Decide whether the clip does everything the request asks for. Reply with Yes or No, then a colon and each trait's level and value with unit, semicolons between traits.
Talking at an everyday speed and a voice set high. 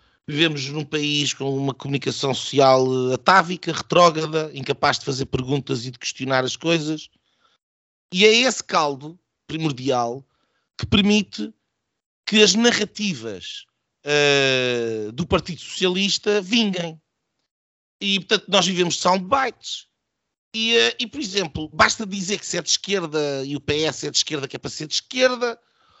No: average, 145 wpm; medium, 155 Hz